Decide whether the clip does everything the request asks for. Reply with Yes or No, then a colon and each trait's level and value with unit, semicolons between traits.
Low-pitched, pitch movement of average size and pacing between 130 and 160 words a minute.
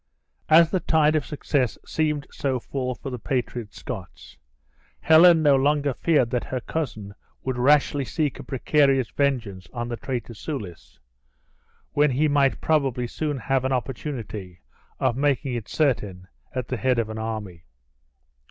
Yes: low, 130 Hz; average, 3.9 semitones; average, 150 wpm